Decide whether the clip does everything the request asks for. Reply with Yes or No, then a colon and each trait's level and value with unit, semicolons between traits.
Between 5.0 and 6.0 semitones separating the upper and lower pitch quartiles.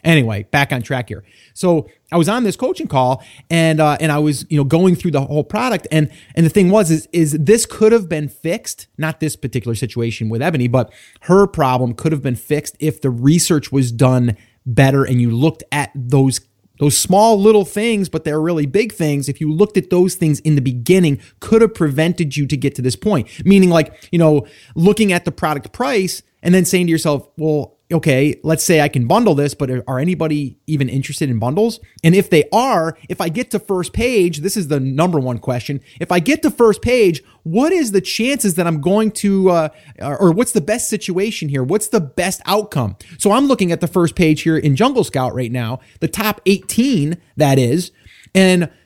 Yes: wide, 5.5 semitones